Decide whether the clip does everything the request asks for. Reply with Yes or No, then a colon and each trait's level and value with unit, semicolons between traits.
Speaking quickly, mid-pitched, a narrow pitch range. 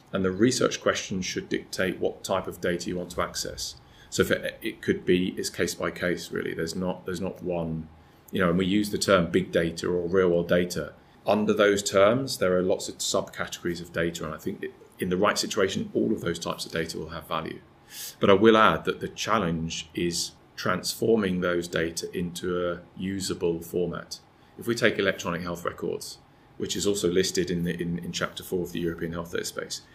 No: fast, 210 wpm; very low, 90 Hz; narrow, 1.8 semitones